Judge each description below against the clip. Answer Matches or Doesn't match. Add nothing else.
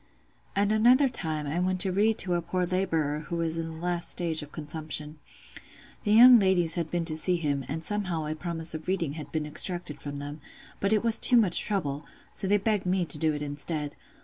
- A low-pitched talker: Doesn't match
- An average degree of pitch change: Matches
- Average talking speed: Doesn't match